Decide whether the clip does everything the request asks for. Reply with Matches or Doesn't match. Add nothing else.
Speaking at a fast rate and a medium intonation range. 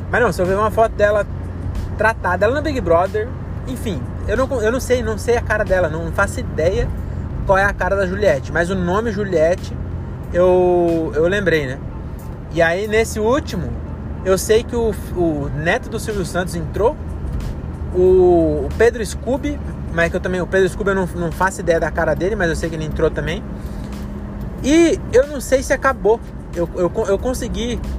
Matches